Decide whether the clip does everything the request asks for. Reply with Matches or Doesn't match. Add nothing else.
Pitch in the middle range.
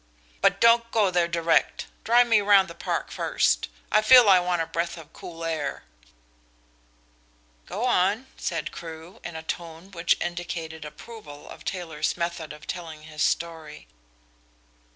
Matches